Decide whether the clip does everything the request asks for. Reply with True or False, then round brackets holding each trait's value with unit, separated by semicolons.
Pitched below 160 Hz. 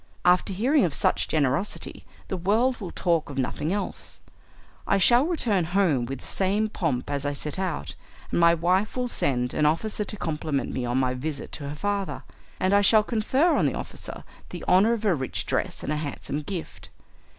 False (180 Hz)